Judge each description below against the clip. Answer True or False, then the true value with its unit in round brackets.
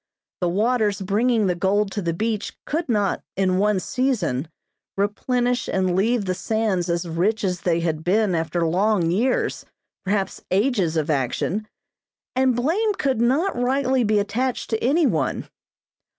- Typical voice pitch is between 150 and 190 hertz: False (205 Hz)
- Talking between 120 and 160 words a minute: True (150 wpm)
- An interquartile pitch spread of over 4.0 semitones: True (5.2 semitones)